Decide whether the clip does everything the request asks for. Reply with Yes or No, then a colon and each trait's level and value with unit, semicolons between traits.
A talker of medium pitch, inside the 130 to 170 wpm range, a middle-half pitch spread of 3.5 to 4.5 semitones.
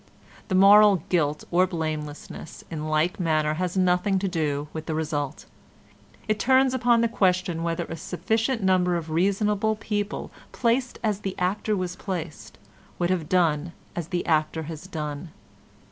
Yes: medium, 180 Hz; average, 155 wpm; average, 4.1 semitones